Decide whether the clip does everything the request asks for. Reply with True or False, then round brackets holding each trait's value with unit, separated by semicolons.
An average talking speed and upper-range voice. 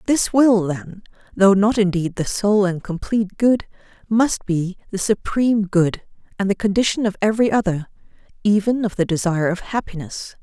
True (160 wpm; 200 Hz)